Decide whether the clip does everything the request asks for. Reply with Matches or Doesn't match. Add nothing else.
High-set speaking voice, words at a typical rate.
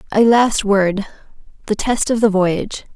Matches